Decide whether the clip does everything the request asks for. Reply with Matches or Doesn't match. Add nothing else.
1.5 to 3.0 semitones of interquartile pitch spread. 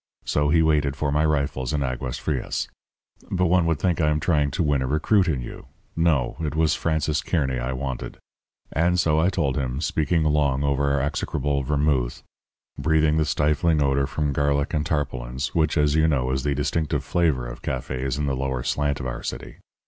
Matches